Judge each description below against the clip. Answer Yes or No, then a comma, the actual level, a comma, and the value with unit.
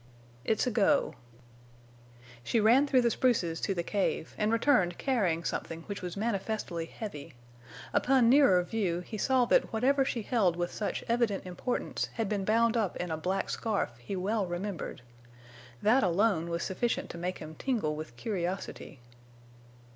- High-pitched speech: Yes, high, 205 Hz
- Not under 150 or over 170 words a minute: Yes, average, 160 wpm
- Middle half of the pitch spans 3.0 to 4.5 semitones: No, average, 4.9 semitones